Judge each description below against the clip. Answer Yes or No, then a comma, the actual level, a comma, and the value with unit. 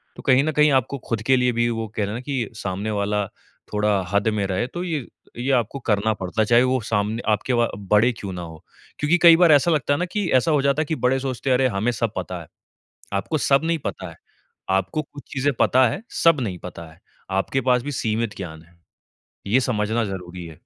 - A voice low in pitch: Yes, low, 115 Hz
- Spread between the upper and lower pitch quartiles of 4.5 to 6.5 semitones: Yes, average, 5.3 semitones